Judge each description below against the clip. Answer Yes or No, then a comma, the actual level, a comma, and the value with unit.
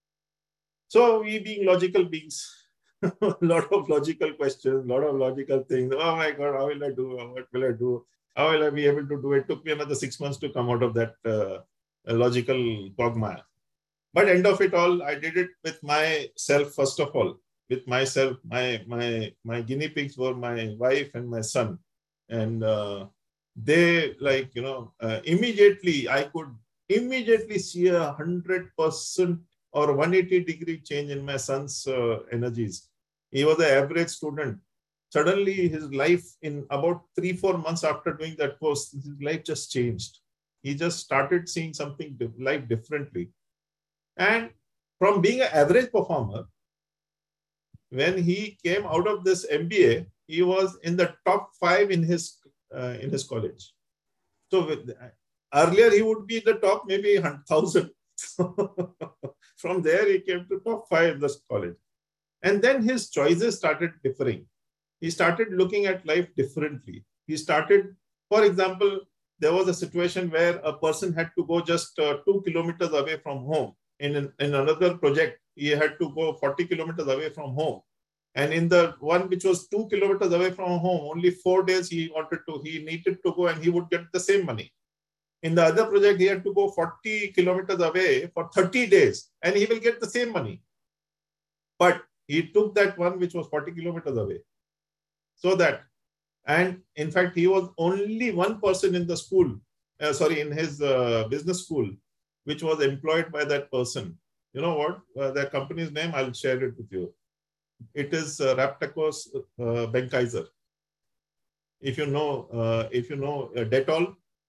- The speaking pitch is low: No, medium, 155 Hz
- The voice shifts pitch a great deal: No, average, 4.8 semitones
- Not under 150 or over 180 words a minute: Yes, average, 175 wpm